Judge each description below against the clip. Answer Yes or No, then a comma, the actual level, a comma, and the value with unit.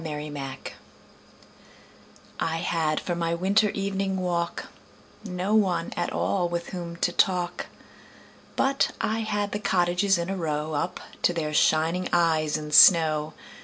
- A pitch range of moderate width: Yes, average, 3.3 semitones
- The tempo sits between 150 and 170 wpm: No, average, 140 wpm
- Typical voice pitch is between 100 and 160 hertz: No, medium, 175 Hz